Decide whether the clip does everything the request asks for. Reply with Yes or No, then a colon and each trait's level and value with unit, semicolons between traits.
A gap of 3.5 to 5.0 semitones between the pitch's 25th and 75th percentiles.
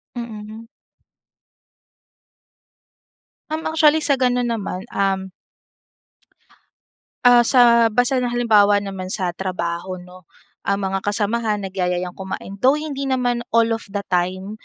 Yes: average, 4.2 semitones